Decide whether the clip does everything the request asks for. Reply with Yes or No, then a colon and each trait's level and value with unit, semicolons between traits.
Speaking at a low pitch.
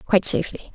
No: high, 190 Hz